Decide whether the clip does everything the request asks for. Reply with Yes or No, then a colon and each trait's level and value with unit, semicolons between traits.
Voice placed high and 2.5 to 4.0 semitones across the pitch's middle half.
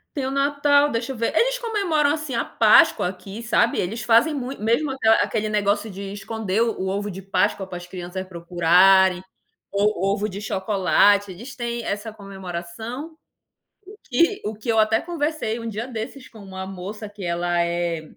No: high, 215 Hz; average, 4.5 semitones